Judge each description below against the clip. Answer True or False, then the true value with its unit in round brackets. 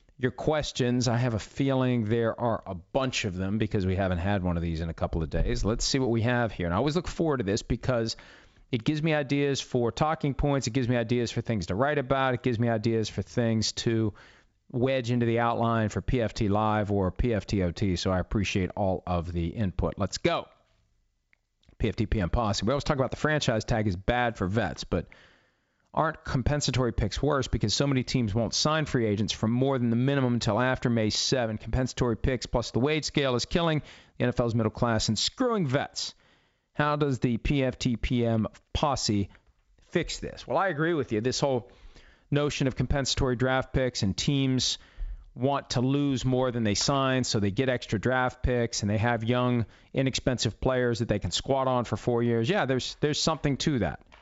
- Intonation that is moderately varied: True (3.7 semitones)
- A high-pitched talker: False (120 Hz)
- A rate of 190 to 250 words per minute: True (205 wpm)